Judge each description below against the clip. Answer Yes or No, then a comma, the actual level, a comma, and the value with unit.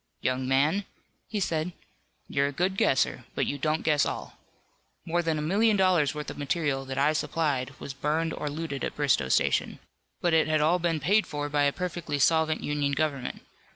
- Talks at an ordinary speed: Yes, average, 190 wpm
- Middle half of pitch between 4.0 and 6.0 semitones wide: No, average, 2.8 semitones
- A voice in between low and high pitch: Yes, medium, 150 Hz